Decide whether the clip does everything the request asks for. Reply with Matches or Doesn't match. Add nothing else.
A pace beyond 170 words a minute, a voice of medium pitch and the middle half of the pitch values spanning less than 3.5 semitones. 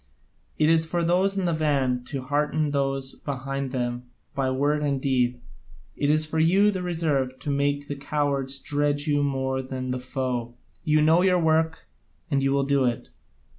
Matches